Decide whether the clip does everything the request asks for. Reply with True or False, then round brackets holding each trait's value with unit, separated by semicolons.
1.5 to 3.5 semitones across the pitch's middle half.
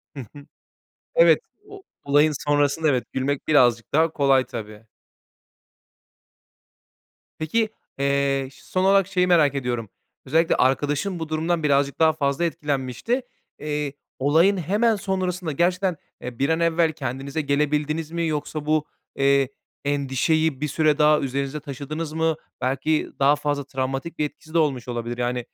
True (2.9 semitones)